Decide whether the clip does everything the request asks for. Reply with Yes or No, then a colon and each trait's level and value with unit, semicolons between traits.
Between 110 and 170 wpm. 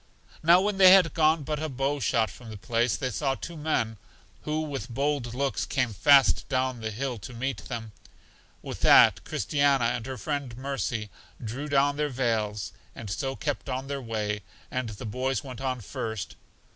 No: average, 185 wpm